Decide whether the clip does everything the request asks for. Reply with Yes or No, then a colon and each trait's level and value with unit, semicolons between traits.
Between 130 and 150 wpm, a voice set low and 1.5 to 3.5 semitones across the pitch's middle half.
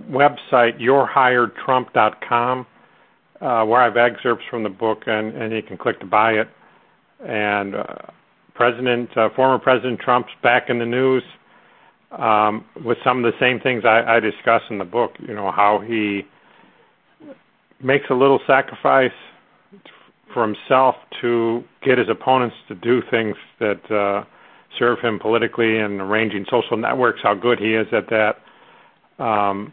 Yes: average, 145 wpm; low, 115 Hz; average, 2.9 semitones